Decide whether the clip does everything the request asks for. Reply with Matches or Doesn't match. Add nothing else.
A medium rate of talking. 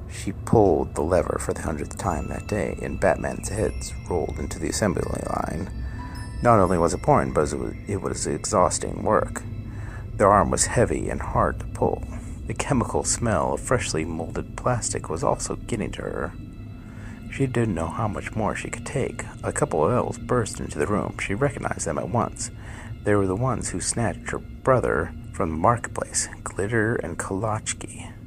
Matches